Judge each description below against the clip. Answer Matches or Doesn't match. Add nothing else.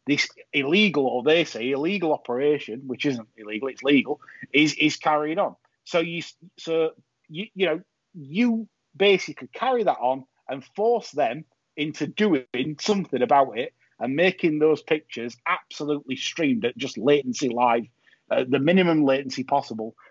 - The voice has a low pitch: Doesn't match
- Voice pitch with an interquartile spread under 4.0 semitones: Doesn't match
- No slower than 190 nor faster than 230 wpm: Doesn't match